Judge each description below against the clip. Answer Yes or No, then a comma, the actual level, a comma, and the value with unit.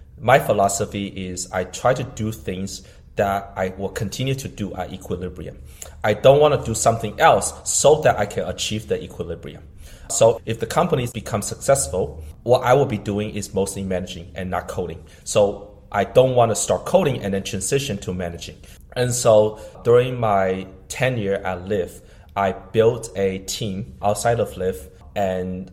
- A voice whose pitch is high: No, low, 100 Hz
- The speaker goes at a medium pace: Yes, average, 175 wpm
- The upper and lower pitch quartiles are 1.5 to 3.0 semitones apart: No, average, 3.4 semitones